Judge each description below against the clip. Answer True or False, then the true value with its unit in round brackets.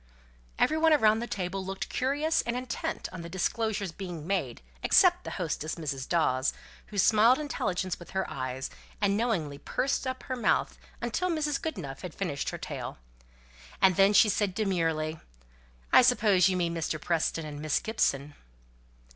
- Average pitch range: False (6.5 semitones)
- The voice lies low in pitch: False (190 Hz)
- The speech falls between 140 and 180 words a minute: True (160 wpm)